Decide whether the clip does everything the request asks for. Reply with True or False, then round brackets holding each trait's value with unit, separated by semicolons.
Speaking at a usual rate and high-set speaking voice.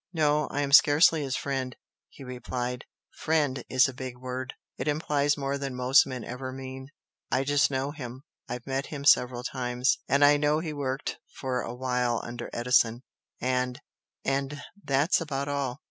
False (170 wpm; 135 Hz)